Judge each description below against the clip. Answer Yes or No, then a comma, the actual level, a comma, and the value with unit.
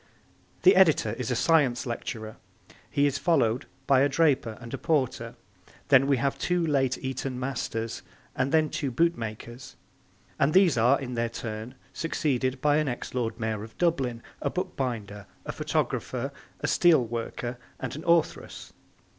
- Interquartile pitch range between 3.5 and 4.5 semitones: Yes, average, 4.2 semitones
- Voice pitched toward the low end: Yes, low, 130 Hz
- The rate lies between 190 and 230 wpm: No, average, 155 wpm